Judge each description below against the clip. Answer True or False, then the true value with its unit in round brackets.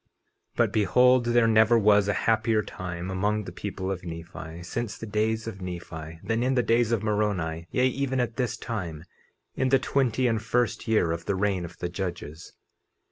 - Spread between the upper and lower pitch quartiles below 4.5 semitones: False (4.8 semitones)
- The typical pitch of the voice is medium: False (105 Hz)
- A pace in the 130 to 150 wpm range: False (190 wpm)